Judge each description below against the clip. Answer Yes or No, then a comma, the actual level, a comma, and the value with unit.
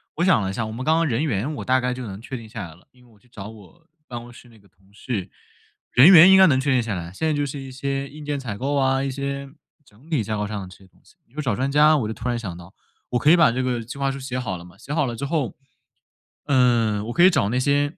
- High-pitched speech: No, low, 125 Hz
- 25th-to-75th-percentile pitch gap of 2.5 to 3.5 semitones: No, average, 4.5 semitones